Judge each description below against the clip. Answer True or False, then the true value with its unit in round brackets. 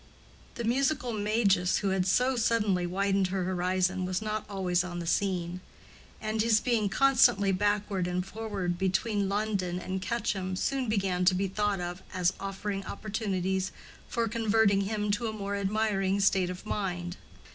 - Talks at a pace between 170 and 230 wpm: False (155 wpm)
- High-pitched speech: True (195 Hz)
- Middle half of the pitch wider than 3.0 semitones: False (2.6 semitones)